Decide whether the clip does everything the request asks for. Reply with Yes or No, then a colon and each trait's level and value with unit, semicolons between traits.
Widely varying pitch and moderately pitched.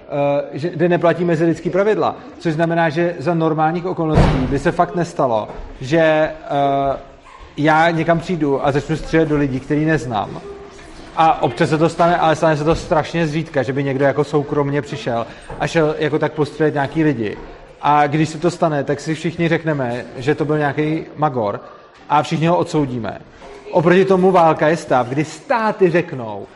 No: narrow, 2.6 semitones; medium, 155 Hz